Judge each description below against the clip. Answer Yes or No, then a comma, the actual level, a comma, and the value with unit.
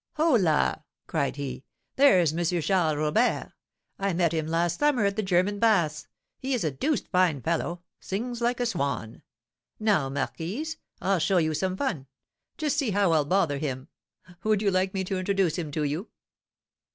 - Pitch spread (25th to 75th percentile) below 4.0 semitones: No, average, 5.1 semitones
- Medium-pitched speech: Yes, medium, 180 Hz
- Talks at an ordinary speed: Yes, average, 170 wpm